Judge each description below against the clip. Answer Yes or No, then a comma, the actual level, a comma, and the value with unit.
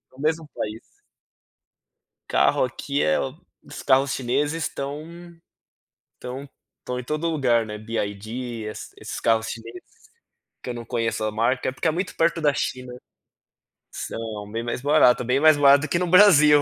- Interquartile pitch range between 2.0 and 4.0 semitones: No, average, 4.5 semitones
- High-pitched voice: No, low, 130 Hz